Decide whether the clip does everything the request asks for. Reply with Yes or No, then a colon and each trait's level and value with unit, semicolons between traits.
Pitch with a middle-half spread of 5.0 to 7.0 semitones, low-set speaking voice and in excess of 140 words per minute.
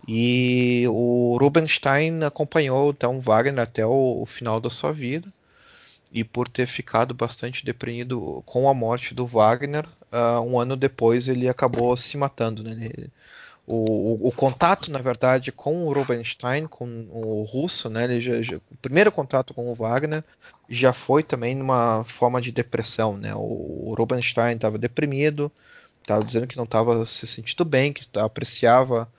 No: average, 2.9 semitones; low, 125 Hz; average, 170 wpm